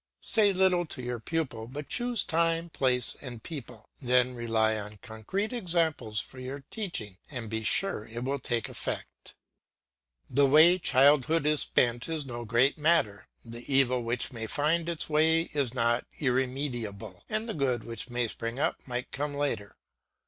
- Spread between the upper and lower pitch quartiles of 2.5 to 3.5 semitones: No, average, 5.3 semitones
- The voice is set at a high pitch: No, low, 130 Hz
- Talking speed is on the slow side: No, average, 165 wpm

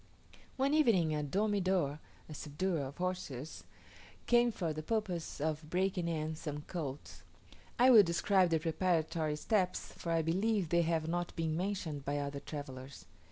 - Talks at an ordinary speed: Yes, average, 155 wpm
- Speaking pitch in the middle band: Yes, medium, 165 Hz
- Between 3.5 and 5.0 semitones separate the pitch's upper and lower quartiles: Yes, average, 3.8 semitones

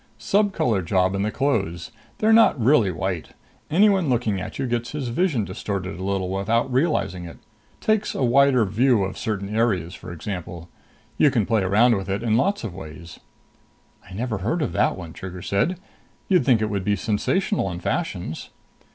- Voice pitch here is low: Yes, low, 105 Hz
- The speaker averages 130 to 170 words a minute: No, average, 180 wpm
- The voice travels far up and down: Yes, wide, 6.1 semitones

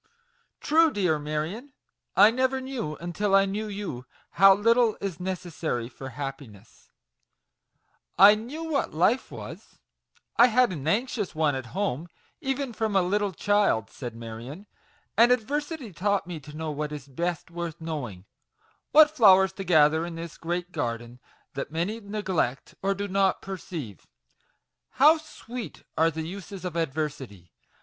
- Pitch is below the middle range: No, medium, 180 Hz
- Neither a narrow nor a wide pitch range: No, wide, 5.9 semitones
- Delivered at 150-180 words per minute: Yes, average, 155 wpm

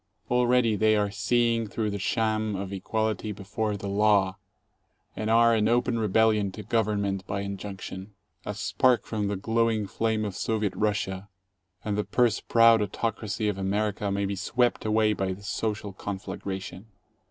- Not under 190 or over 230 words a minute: No, average, 160 wpm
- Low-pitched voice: Yes, low, 105 Hz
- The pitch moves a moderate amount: No, narrow, 2.1 semitones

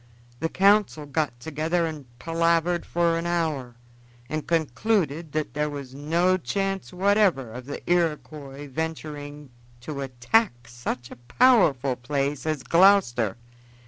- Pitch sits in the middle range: Yes, medium, 155 Hz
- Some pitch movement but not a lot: Yes, average, 4.2 semitones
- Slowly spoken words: Yes, slow, 125 wpm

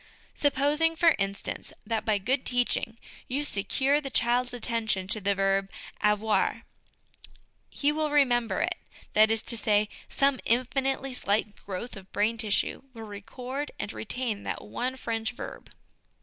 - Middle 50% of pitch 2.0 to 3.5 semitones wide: No, average, 4.2 semitones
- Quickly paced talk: No, average, 145 wpm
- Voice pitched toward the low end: No, high, 230 Hz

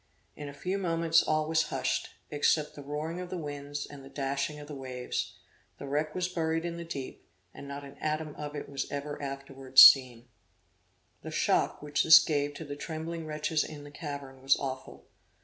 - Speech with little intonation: Yes, narrow, 2.3 semitones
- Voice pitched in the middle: Yes, medium, 145 Hz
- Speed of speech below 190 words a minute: No, average, 195 wpm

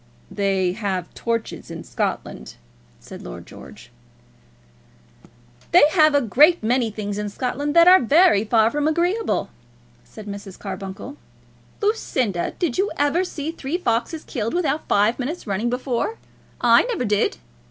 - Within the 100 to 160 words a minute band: Yes, average, 140 wpm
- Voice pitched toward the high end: Yes, high, 245 Hz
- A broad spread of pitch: Yes, wide, 7.3 semitones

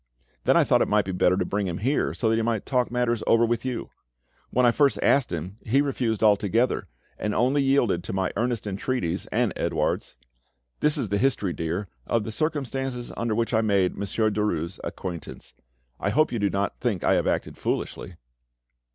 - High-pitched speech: No, low, 110 Hz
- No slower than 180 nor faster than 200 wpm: Yes, average, 195 wpm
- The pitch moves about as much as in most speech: Yes, average, 4.0 semitones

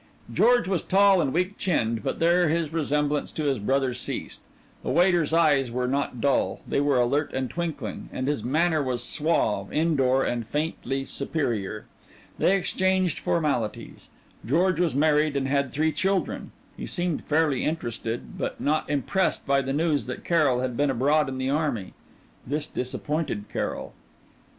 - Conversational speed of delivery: Yes, average, 160 wpm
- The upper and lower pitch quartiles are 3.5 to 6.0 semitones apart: Yes, average, 4.1 semitones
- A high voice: No, medium, 145 Hz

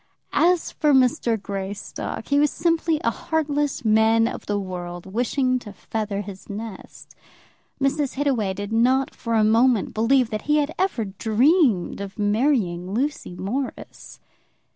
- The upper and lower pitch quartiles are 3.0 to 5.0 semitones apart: No, wide, 5.5 semitones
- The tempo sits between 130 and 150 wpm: Yes, average, 140 wpm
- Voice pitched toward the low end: No, high, 230 Hz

